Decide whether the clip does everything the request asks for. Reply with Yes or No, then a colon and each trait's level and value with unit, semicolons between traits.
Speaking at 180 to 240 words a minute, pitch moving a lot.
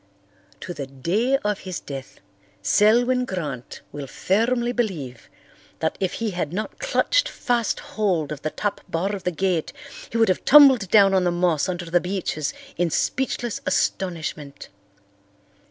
No: average, 155 wpm; wide, 5.8 semitones